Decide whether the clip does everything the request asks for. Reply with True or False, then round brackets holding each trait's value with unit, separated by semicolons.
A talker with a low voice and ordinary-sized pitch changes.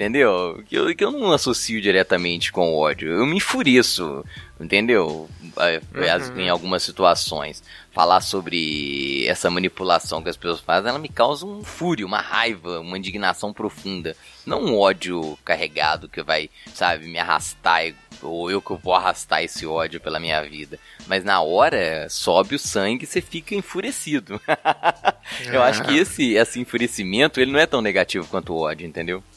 False (90 Hz; 6.4 semitones)